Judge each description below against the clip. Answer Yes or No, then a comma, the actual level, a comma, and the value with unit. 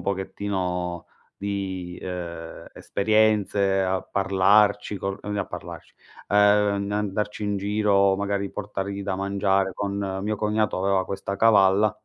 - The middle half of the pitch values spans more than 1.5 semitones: No, narrow, 1.2 semitones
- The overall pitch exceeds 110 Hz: No, low, 100 Hz